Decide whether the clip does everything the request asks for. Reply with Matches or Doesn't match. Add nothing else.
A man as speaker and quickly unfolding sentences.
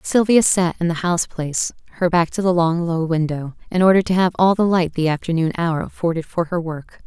Doesn't match